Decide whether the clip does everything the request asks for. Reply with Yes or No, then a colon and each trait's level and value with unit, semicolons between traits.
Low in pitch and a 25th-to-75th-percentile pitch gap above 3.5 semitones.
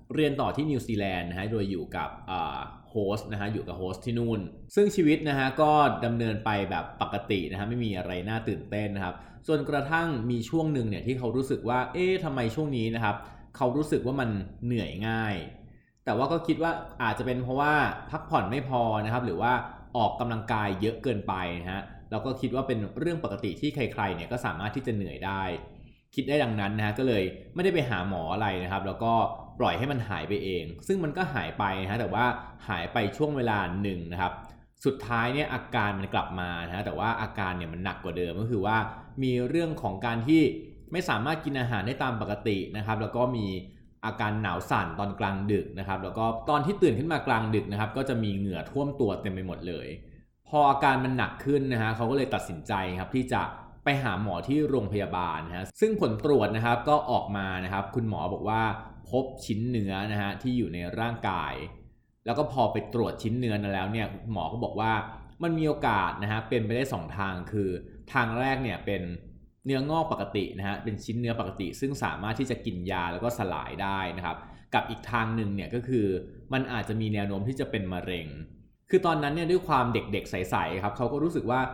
Yes: low, 110 Hz; average, 4.5 semitones